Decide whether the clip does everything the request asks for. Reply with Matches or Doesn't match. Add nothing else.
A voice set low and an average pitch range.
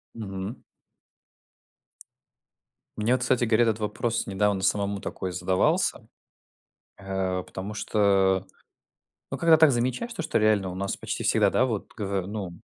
Matches